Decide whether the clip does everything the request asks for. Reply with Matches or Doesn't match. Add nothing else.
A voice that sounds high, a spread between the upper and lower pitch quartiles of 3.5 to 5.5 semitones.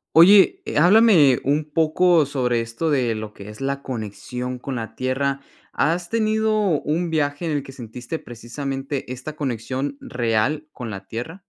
Doesn't match